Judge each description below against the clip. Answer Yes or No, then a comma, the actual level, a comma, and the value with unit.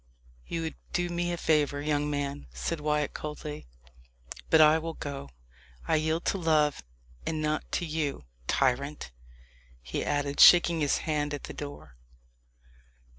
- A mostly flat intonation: Yes, narrow, 2.0 semitones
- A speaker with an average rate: Yes, average, 145 wpm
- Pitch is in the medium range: Yes, medium, 150 Hz